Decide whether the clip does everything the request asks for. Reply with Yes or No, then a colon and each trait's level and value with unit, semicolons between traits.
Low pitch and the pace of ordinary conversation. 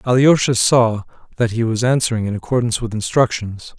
Yes: low, 115 Hz; average, 160 wpm